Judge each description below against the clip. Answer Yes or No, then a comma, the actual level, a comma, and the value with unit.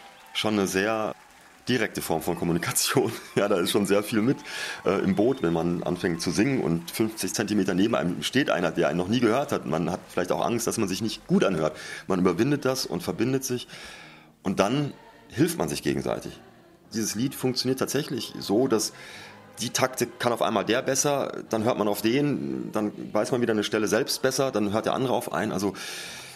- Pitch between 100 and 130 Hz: Yes, low, 110 Hz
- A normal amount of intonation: Yes, average, 4.2 semitones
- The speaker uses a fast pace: Yes, fast, 205 wpm